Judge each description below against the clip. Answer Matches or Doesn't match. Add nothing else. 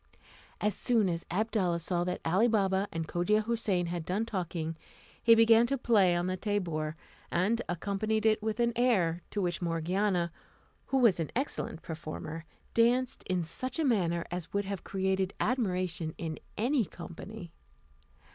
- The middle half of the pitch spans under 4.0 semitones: Doesn't match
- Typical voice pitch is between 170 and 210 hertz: Matches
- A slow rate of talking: Doesn't match